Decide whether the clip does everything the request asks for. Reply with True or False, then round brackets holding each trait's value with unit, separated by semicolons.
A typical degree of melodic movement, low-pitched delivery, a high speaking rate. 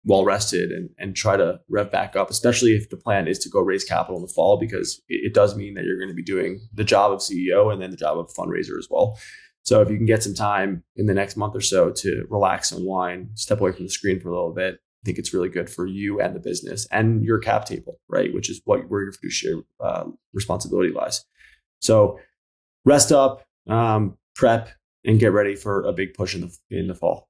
True (3.4 semitones; 105 Hz; 245 wpm)